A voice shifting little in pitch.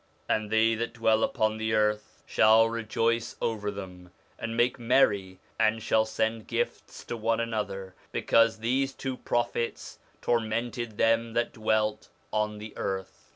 Yes: narrow, 1.4 semitones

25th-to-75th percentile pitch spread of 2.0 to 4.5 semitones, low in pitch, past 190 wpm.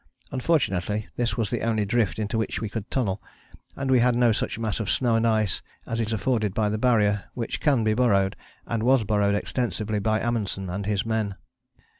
Yes: narrow, 2.4 semitones; low, 110 Hz; average, 200 wpm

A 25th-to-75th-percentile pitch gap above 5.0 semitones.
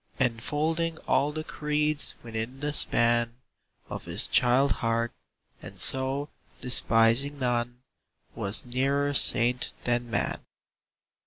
No: average, 3.4 semitones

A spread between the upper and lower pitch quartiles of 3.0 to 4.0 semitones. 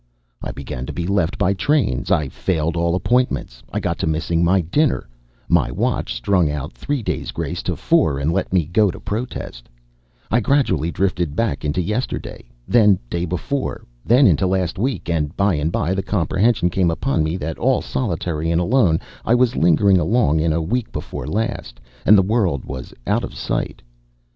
No: average, 5.2 semitones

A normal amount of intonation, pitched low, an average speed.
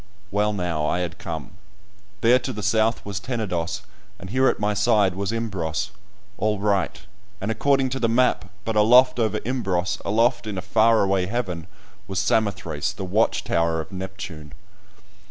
Yes: average, 3.6 semitones; low, 105 Hz; average, 165 wpm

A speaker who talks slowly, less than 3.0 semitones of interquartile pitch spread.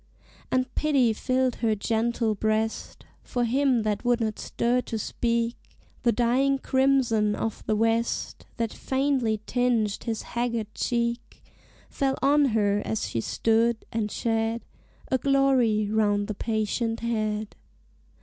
Yes: slow, 130 wpm; narrow, 2.4 semitones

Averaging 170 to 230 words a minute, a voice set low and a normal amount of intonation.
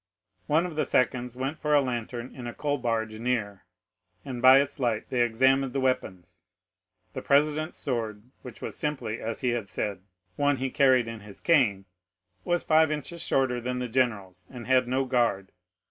Yes: average, 180 wpm; low, 125 Hz; average, 3.3 semitones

